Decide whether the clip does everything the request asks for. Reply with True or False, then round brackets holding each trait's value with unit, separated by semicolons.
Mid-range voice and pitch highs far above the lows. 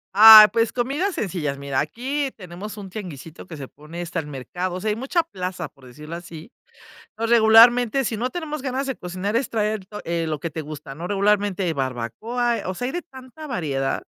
False (200 Hz; 6.7 semitones)